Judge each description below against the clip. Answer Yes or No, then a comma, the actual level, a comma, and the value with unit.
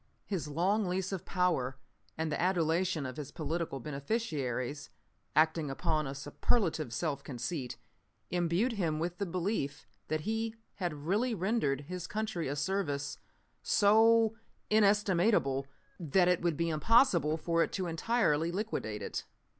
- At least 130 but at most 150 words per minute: Yes, average, 140 wpm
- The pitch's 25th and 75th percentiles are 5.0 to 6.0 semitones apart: Yes, average, 5.3 semitones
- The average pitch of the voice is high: No, medium, 170 Hz